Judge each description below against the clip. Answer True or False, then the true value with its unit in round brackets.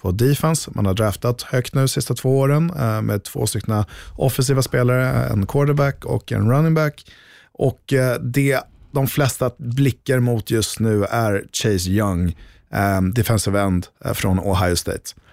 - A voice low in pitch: True (120 Hz)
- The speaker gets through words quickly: False (150 wpm)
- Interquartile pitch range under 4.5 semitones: False (4.9 semitones)